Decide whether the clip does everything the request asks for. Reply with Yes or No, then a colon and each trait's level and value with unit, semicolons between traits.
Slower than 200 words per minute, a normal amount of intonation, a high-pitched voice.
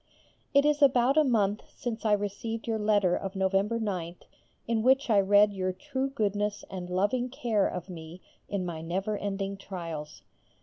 Yes: average, 170 wpm; average, 3.6 semitones; high, 205 Hz